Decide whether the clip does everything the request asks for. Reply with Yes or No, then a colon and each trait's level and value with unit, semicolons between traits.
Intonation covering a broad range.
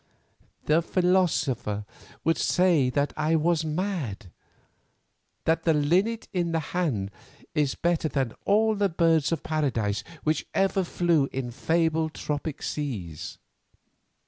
No: average, 4.0 semitones